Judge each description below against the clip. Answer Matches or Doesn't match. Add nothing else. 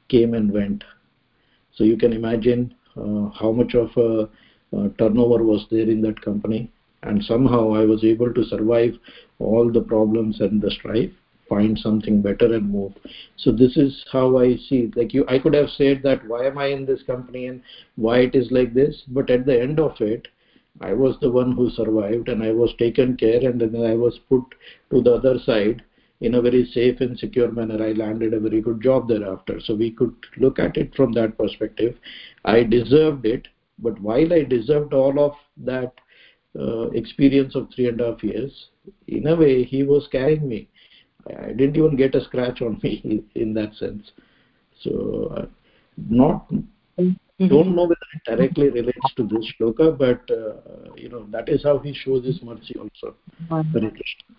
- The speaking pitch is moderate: Doesn't match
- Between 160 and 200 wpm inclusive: Matches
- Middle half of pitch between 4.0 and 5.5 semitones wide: Doesn't match